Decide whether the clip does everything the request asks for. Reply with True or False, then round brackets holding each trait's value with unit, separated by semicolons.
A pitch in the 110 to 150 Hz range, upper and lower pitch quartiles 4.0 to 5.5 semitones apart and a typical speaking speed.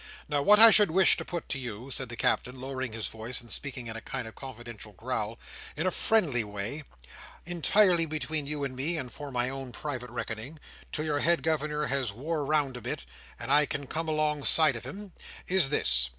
False (140 Hz; 4.3 semitones; 210 wpm)